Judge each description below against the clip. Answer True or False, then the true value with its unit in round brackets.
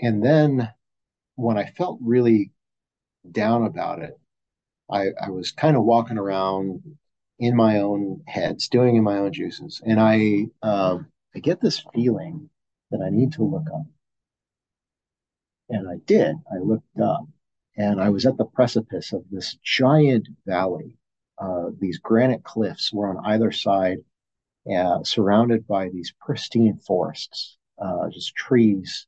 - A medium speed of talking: True (145 wpm)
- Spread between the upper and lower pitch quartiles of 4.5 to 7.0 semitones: False (3.7 semitones)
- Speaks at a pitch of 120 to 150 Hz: False (110 Hz)